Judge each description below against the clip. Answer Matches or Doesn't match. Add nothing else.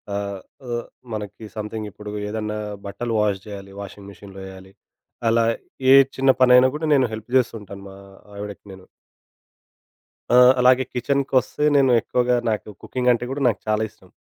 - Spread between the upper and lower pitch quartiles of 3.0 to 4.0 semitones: Matches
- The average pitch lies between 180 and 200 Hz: Doesn't match